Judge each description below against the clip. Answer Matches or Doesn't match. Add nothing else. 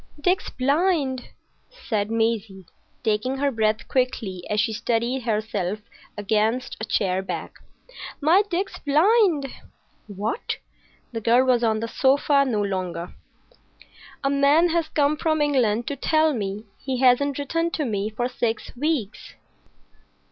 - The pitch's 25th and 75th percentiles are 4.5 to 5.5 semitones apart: Matches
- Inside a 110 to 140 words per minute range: Matches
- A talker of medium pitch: Doesn't match